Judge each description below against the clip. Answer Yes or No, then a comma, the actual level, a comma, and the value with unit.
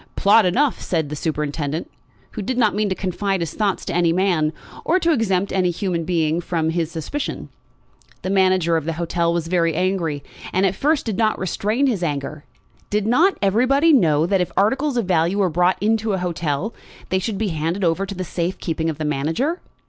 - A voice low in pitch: No, medium, 185 Hz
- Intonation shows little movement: No, average, 4.3 semitones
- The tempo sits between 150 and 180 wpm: No, average, 200 wpm